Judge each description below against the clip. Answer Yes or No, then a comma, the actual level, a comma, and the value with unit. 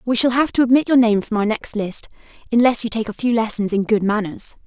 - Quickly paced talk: Yes, fast, 255 wpm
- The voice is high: Yes, high, 225 Hz